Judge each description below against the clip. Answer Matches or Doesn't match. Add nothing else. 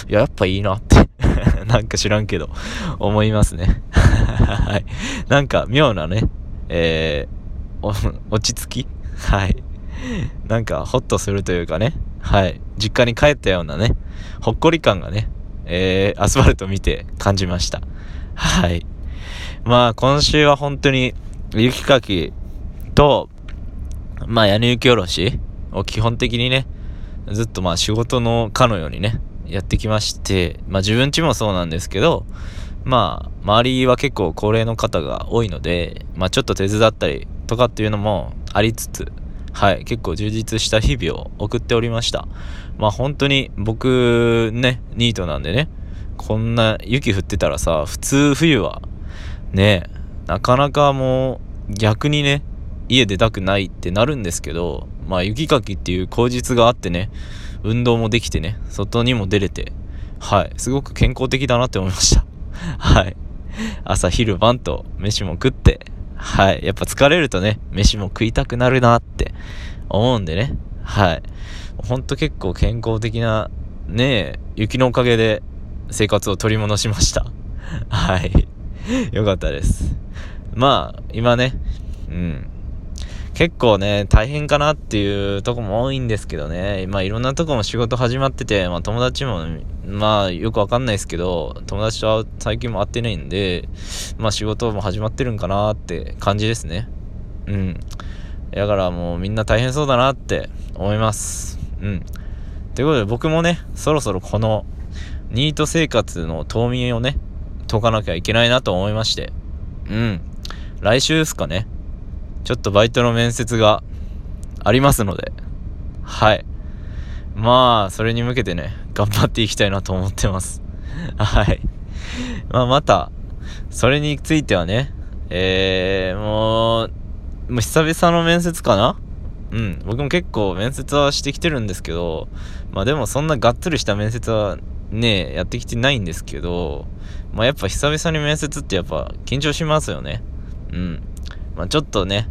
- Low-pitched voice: Matches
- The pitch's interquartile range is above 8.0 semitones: Doesn't match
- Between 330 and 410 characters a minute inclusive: Doesn't match